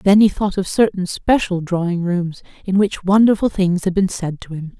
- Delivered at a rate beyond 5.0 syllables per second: No, 4.9 syllables/s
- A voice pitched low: No, medium, 185 Hz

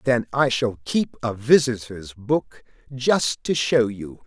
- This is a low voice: Yes, low, 120 Hz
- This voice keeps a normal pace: Yes, average, 155 wpm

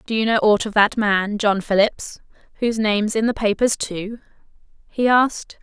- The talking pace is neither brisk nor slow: Yes, average, 180 wpm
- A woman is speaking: Yes, female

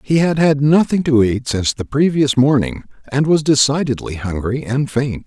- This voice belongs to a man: Yes, male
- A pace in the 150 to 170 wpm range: No, average, 180 wpm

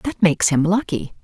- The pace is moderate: Yes, average, 195 wpm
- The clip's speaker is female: Yes, female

